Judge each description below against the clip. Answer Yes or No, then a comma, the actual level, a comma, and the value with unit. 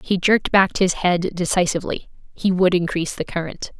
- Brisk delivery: No, average, 175 wpm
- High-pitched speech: No, medium, 180 Hz